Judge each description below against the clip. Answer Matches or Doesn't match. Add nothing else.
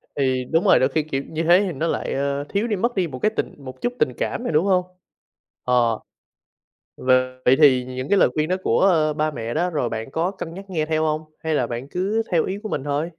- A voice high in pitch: Doesn't match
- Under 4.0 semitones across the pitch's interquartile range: Doesn't match